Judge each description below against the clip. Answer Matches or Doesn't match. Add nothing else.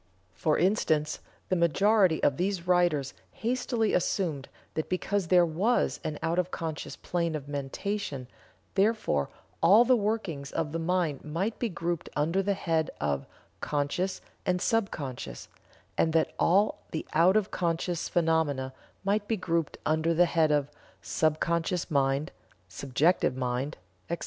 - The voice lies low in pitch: Doesn't match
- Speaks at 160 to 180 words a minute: Doesn't match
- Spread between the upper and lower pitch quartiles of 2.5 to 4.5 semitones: Matches